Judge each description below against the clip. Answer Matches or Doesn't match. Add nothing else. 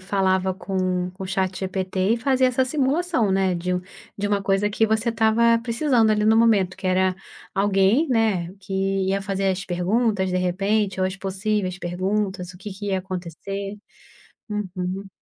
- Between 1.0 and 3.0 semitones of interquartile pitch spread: Matches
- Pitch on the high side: Matches